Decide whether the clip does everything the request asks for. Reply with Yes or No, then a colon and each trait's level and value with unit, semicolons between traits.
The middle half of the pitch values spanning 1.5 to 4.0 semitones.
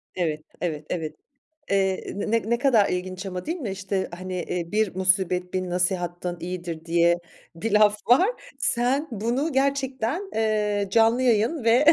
No: average, 4.8 semitones